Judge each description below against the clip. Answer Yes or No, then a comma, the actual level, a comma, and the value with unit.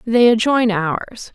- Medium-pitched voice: No, high, 225 Hz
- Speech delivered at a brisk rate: No, slow, 135 wpm